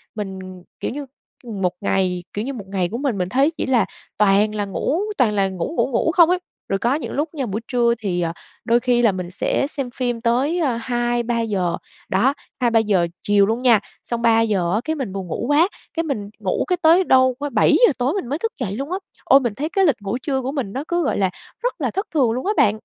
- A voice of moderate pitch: No, high, 240 Hz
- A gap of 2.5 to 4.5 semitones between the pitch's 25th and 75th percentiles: No, wide, 5.6 semitones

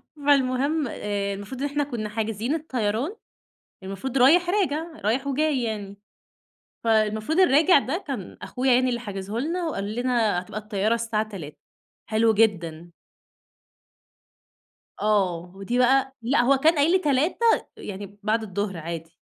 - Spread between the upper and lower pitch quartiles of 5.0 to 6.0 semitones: Yes, average, 5.3 semitones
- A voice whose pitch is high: Yes, high, 230 Hz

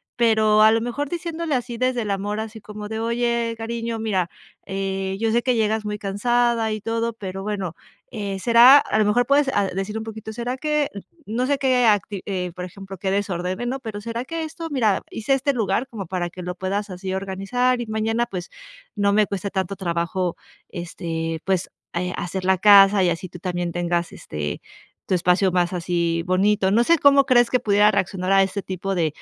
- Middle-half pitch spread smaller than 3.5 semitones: No, average, 3.9 semitones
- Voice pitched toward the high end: Yes, high, 210 Hz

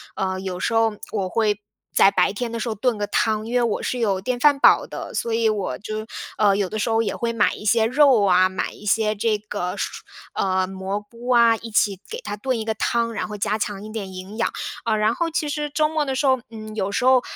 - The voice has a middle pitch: No, high, 220 Hz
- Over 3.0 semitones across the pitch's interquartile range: No, narrow, 2.6 semitones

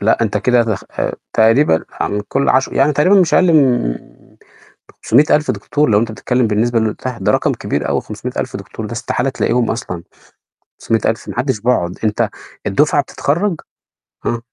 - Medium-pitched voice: No, low, 120 Hz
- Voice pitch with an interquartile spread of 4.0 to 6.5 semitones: Yes, average, 4.3 semitones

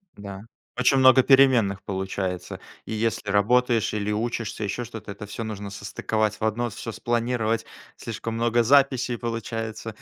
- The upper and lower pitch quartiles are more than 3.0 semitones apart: No, average, 2.7 semitones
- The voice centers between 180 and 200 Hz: No, low, 115 Hz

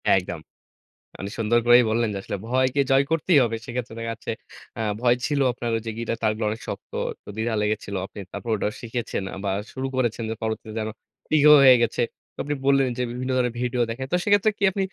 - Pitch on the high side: No, low, 120 Hz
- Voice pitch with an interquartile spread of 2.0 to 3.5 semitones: Yes, average, 2.8 semitones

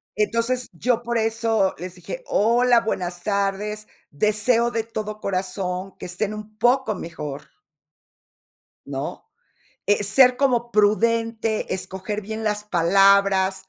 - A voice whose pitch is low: No, high, 210 Hz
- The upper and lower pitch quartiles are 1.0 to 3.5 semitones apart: Yes, average, 3.1 semitones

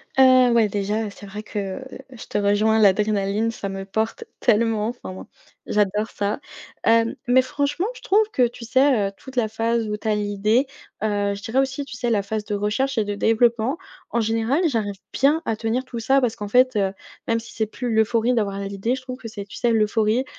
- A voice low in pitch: No, high, 220 Hz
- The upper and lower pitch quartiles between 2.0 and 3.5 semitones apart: Yes, average, 3.2 semitones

